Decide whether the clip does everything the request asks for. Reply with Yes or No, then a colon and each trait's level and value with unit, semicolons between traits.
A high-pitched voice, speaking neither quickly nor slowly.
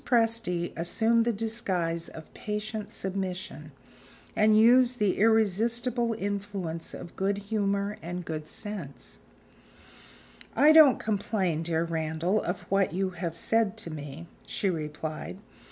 No: high, 195 Hz; slow, 120 wpm